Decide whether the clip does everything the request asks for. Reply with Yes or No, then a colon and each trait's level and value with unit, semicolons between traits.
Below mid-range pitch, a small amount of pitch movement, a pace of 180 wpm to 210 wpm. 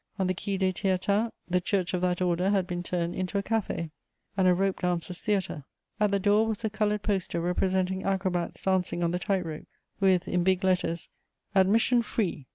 No: medium, 185 Hz; narrow, 2.0 semitones; average, 195 wpm